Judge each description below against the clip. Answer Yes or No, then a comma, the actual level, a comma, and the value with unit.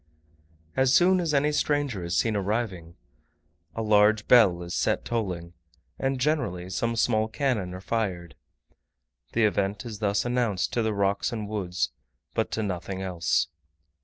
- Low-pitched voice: Yes, low, 105 Hz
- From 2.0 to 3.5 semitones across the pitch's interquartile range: No, average, 4.4 semitones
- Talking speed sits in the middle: Yes, average, 150 wpm